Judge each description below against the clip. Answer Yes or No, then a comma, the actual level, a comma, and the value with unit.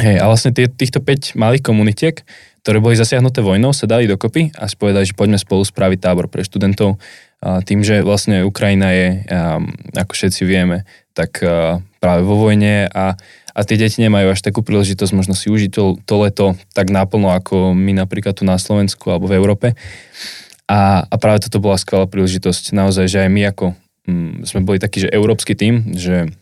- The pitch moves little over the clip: Yes, narrow, 2.2 semitones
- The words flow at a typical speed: No, fast, 180 wpm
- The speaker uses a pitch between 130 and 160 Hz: No, low, 100 Hz